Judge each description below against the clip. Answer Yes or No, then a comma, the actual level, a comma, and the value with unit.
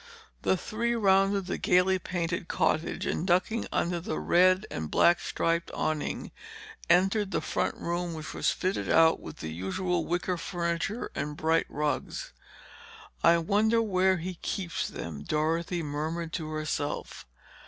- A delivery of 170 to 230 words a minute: No, average, 145 wpm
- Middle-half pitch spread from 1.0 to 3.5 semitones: Yes, average, 3.0 semitones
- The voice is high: No, medium, 170 Hz